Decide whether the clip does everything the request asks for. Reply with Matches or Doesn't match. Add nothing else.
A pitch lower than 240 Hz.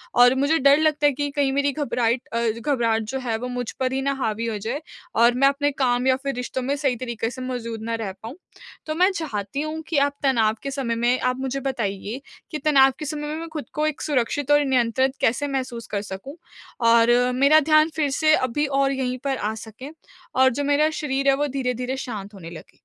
Doesn't match